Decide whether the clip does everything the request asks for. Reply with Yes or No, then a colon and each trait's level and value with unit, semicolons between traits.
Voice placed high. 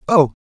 No: medium, 150 Hz